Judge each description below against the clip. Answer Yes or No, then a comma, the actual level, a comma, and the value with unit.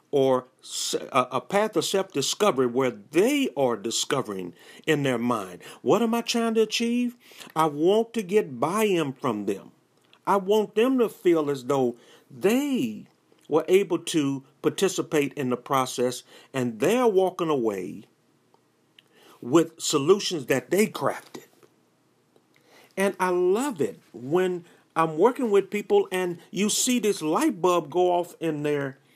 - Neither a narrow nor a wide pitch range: No, wide, 7.0 semitones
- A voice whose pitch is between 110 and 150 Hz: No, medium, 175 Hz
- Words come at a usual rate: Yes, average, 145 wpm